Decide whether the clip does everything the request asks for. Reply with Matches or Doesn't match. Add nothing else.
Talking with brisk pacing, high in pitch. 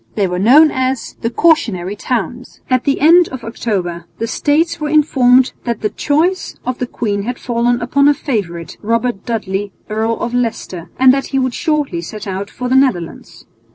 Doesn't match